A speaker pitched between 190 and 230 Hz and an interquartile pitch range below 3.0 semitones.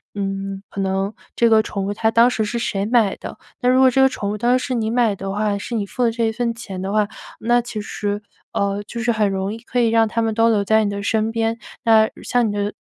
Yes: high, 220 Hz; narrow, 2.5 semitones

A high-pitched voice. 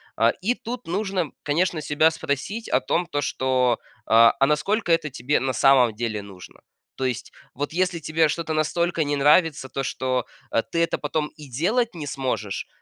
No: medium, 150 Hz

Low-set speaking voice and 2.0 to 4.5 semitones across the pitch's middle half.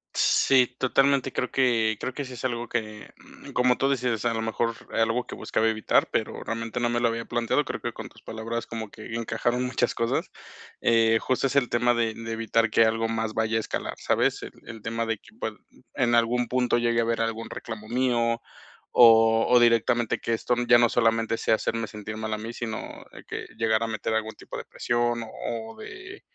No: low, 115 Hz; narrow, 1.2 semitones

